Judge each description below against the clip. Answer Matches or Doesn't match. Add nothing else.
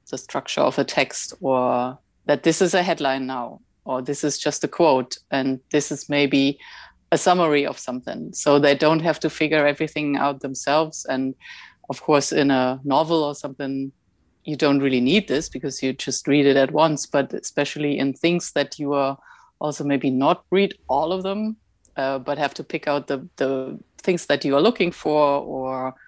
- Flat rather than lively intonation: Matches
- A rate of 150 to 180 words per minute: Doesn't match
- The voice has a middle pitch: Matches